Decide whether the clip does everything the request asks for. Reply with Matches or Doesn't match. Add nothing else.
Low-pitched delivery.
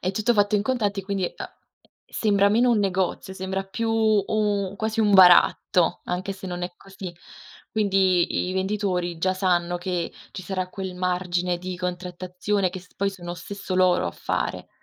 Doesn't match